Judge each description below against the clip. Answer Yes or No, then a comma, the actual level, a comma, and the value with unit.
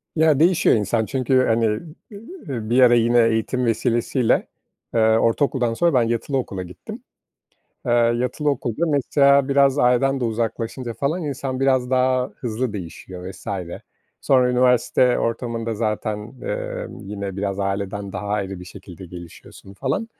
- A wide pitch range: No, average, 3.9 semitones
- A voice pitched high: No, low, 120 Hz